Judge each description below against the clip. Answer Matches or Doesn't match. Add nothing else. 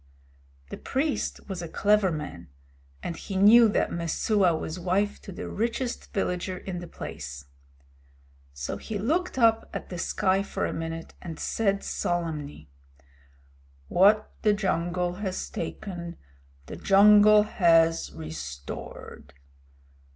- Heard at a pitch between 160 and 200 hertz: Matches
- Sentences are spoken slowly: Matches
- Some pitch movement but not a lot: Matches